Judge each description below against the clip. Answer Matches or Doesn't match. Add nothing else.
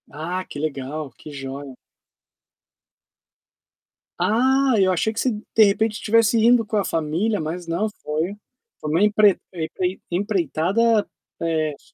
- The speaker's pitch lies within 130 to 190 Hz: Matches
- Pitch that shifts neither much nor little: Doesn't match